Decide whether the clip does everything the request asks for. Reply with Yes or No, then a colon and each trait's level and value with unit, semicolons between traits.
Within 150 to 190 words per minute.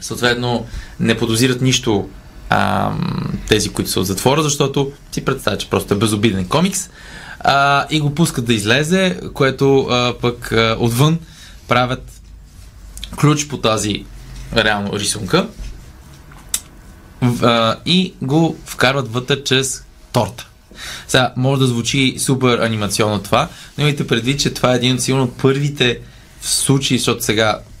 No: average, 135 wpm